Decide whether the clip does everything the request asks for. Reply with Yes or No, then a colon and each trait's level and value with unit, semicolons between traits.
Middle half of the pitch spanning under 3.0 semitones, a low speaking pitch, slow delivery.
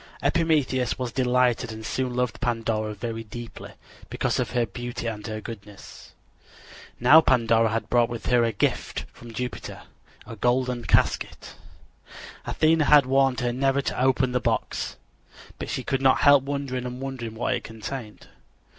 No: narrow, 2.4 semitones; low, 125 Hz; average, 160 wpm